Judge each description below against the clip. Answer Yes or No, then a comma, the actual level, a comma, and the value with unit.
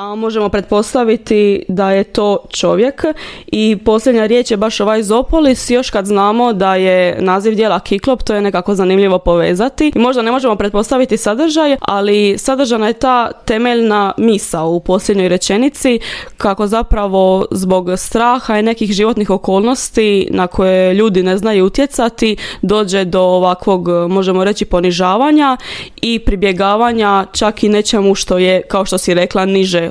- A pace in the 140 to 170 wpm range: Yes, average, 150 wpm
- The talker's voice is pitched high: Yes, high, 210 Hz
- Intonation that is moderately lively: Yes, average, 3.4 semitones